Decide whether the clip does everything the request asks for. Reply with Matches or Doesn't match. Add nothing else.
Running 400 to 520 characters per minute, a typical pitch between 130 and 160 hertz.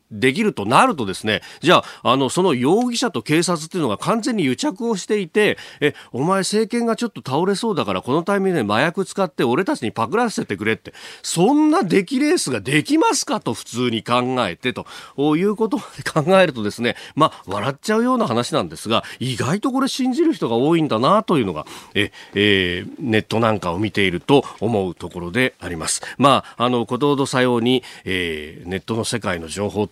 Matches